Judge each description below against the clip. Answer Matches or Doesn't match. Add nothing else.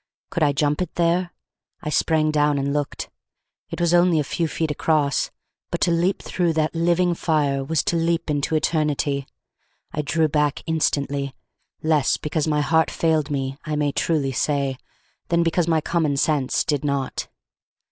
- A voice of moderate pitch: Matches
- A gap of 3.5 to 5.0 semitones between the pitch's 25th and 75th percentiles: Doesn't match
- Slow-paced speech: Doesn't match